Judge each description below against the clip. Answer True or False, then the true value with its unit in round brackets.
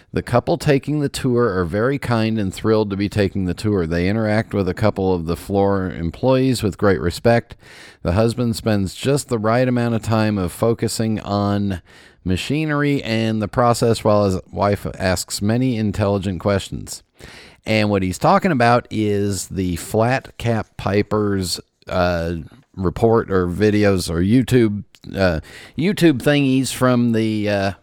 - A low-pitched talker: True (105 Hz)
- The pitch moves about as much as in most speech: True (3.6 semitones)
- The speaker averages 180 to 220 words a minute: False (155 wpm)